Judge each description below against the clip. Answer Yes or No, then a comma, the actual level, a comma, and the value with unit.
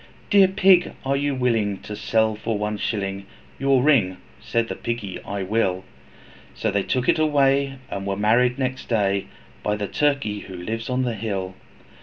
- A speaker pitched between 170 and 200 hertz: No, low, 115 Hz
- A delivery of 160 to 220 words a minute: Yes, average, 175 wpm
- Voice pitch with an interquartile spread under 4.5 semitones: No, average, 5.0 semitones